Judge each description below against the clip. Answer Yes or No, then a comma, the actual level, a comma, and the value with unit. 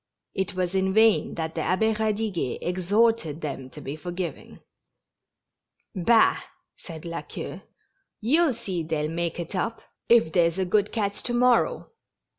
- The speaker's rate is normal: Yes, average, 145 wpm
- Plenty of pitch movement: No, average, 4.8 semitones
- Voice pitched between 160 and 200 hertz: Yes, medium, 185 Hz